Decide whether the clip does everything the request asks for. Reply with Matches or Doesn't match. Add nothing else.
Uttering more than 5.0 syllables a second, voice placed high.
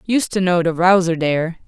Doesn't match